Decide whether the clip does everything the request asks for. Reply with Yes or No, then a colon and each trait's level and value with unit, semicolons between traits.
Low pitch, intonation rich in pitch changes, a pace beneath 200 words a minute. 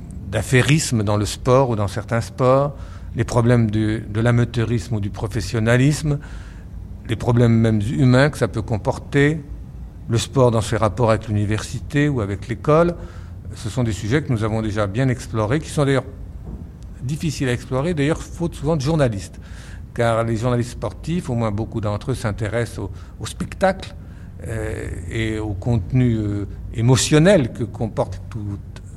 No: low, 115 Hz; average, 3.6 semitones; average, 160 wpm